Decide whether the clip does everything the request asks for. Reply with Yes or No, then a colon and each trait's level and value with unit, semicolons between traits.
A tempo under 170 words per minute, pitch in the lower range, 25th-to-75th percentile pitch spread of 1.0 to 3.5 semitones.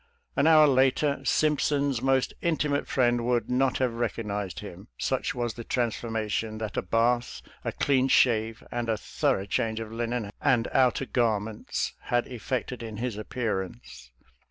Yes: average, 150 wpm; low, 120 Hz; average, 3.1 semitones